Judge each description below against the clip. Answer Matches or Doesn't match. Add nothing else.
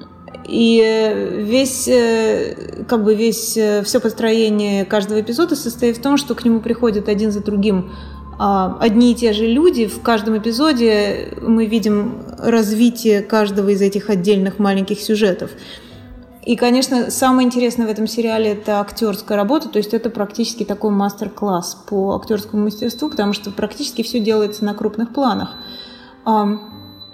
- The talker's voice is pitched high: Matches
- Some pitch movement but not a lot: Doesn't match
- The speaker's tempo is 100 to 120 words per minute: Doesn't match